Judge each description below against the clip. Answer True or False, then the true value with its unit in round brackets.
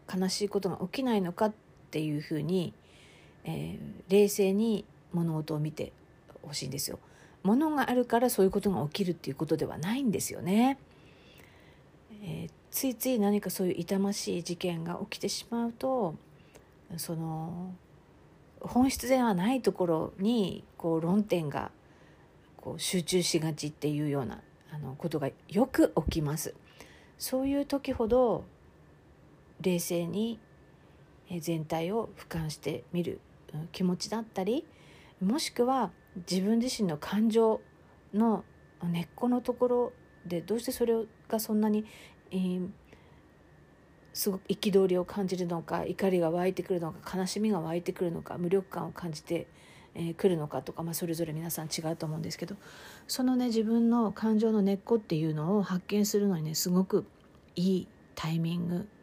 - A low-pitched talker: False (185 Hz)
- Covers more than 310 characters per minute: False (295 characters per minute)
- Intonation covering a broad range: False (4.4 semitones)